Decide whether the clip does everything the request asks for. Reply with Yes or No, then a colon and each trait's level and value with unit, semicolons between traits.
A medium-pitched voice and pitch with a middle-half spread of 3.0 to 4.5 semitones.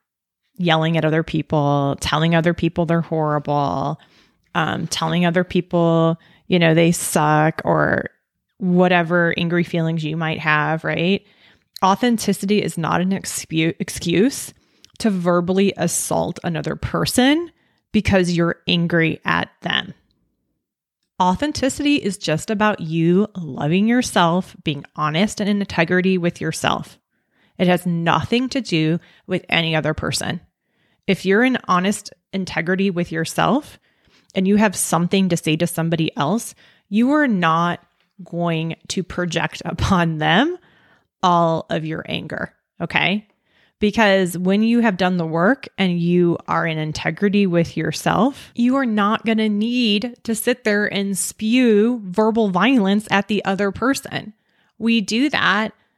Yes: medium, 180 Hz; average, 4.0 semitones